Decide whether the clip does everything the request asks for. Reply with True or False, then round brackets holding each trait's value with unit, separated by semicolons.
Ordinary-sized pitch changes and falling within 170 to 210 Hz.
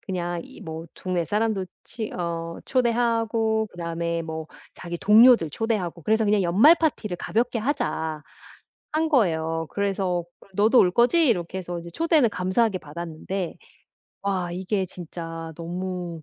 True (4.7 semitones; 185 Hz)